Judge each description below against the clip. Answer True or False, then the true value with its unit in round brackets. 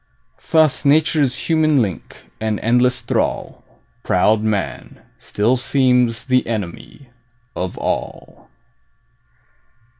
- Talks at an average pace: False (90 wpm)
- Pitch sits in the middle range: False (125 Hz)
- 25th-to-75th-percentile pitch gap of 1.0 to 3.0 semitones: False (4.3 semitones)